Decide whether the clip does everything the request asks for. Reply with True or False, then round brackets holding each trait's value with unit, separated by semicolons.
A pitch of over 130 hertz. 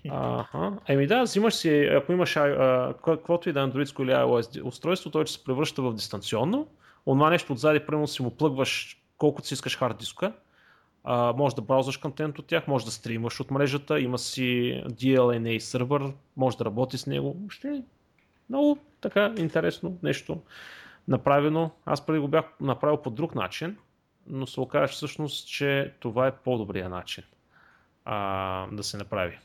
True (140 Hz)